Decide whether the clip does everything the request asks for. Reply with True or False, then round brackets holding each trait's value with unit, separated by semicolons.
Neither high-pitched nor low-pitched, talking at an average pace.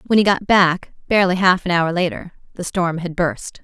False (180 Hz; 215 wpm)